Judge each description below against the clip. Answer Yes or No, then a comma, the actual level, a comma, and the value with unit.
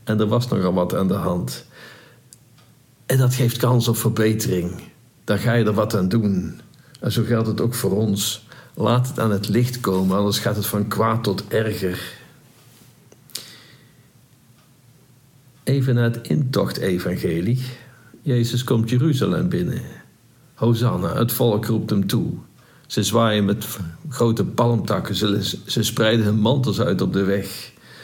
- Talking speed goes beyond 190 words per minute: No, average, 150 wpm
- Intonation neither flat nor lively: Yes, average, 3.1 semitones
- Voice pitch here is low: Yes, low, 115 Hz